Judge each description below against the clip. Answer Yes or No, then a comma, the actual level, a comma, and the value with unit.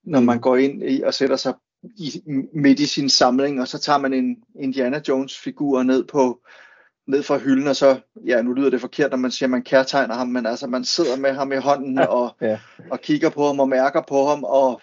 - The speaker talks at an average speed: No, fast, 230 wpm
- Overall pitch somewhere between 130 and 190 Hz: Yes, low, 135 Hz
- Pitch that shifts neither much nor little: No, narrow, 1.8 semitones